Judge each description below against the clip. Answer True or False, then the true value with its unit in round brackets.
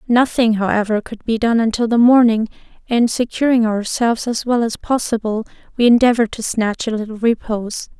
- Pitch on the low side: False (225 Hz)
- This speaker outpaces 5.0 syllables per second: True (5.5 syllables/s)